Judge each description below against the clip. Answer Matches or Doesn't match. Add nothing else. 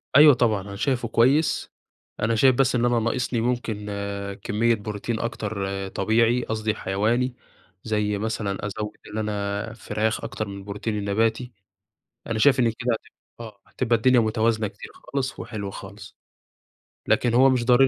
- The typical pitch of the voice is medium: Doesn't match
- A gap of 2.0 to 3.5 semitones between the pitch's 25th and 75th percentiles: Matches